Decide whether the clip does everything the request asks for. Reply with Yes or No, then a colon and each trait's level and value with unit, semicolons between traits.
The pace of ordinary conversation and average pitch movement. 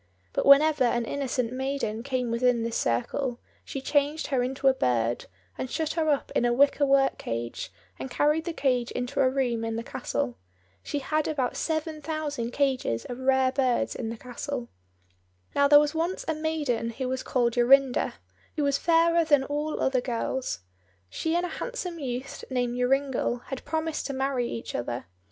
Yes: average, 180 wpm; average, 3.3 semitones